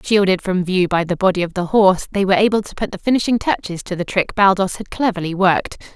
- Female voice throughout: Yes, female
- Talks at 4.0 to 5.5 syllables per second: No, 6.2 syllables/s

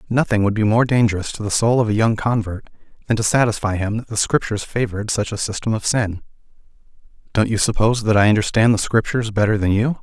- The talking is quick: Yes, fast, 215 wpm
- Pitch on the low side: Yes, low, 110 Hz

